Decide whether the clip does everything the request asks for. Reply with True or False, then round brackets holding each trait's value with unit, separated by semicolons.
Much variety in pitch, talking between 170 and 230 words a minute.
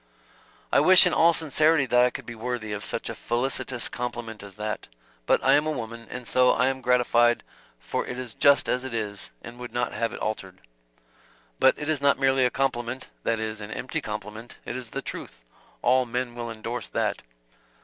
False (2.6 semitones; 200 wpm)